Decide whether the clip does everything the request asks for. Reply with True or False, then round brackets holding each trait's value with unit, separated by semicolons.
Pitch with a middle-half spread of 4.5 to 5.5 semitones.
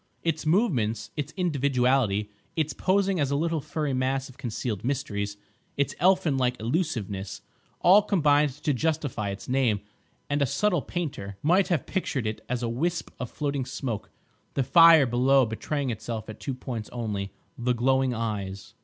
True (5.2 semitones)